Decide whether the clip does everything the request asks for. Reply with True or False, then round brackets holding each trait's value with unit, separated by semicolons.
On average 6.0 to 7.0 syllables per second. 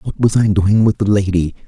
False (5.2 syllables/s)